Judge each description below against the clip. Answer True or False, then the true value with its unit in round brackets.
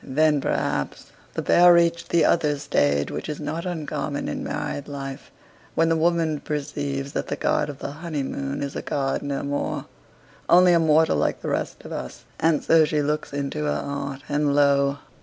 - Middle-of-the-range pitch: True (145 Hz)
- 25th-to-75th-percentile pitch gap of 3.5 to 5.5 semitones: False (2.4 semitones)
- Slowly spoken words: False (185 wpm)